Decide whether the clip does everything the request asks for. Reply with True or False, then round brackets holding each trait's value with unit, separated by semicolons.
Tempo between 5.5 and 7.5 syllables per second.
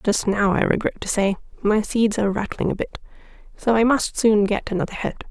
True (5.6 syllables/s)